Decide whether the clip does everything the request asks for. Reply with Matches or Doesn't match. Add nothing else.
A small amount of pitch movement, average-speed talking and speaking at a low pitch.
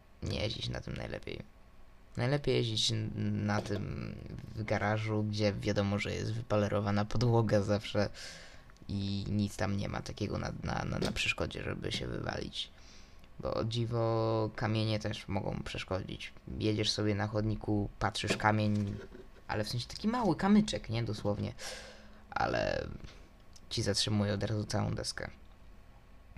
Matches